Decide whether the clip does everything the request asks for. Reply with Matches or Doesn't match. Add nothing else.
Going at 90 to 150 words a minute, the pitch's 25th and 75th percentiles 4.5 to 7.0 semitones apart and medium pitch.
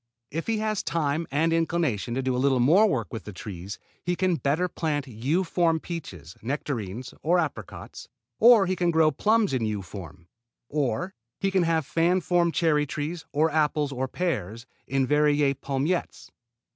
Doesn't match